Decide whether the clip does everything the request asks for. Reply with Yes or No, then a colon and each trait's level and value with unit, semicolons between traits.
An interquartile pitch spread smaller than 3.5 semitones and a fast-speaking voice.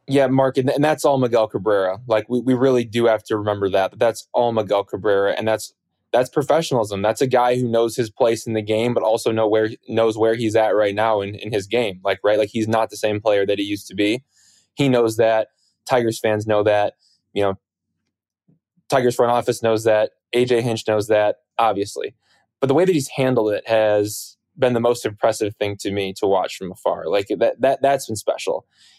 Yes: average, 2.8 semitones; fast, 220 wpm